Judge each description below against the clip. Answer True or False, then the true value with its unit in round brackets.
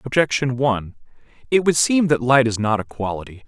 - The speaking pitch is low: True (130 Hz)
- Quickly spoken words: False (190 wpm)